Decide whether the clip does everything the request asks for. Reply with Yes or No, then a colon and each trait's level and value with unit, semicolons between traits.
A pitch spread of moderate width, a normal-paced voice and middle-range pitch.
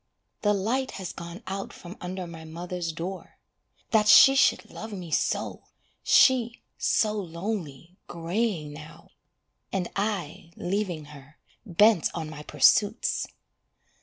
No: average, 4.2 semitones; slow, 125 wpm; medium, 180 Hz